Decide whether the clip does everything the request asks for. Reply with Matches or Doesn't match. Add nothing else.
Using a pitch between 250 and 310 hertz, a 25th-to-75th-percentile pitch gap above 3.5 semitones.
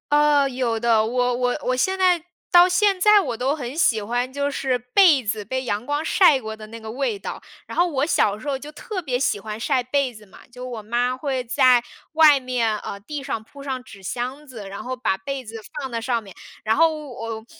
Matches